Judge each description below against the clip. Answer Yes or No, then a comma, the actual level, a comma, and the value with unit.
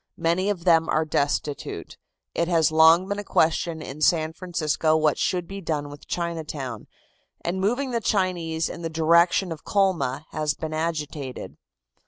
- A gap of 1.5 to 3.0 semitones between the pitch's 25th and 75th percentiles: Yes, narrow, 2.4 semitones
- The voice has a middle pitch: Yes, medium, 165 Hz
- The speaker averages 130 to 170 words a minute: Yes, average, 160 wpm